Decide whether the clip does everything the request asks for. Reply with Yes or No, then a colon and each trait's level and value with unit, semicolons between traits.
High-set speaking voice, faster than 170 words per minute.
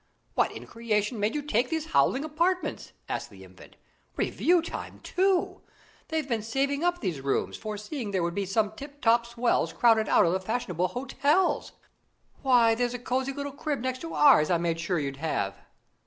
Yes: high, 240 Hz; average, 185 wpm